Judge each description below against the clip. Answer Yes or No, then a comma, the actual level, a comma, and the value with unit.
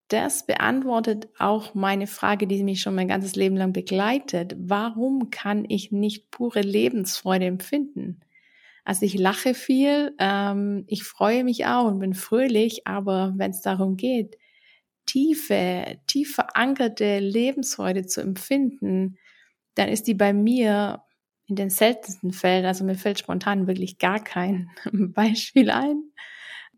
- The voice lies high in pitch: Yes, high, 205 Hz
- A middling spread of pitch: Yes, average, 4.2 semitones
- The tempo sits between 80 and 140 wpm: Yes, average, 135 wpm